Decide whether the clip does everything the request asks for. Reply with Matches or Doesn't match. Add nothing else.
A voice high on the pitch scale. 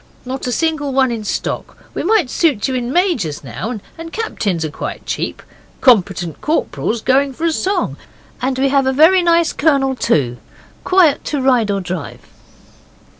Matches